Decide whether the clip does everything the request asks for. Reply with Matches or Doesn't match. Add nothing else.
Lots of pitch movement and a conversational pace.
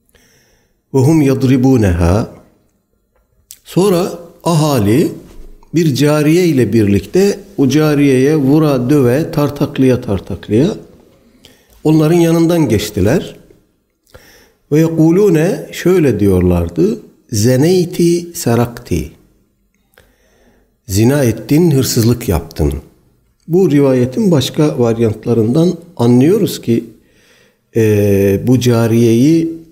Doesn't match